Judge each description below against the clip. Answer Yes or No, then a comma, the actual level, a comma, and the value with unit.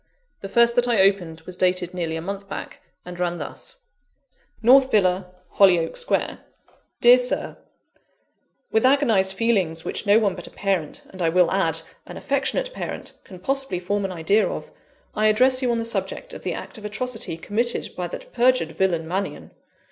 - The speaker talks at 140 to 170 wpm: No, average, 180 wpm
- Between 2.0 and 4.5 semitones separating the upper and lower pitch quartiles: No, average, 5.0 semitones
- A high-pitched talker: Yes, high, 200 Hz